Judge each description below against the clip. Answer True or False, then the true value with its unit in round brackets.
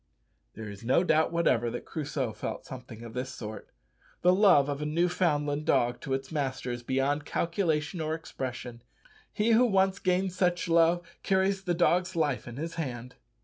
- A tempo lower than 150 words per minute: False (175 wpm)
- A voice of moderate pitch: True (150 Hz)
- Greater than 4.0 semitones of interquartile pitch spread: True (5.5 semitones)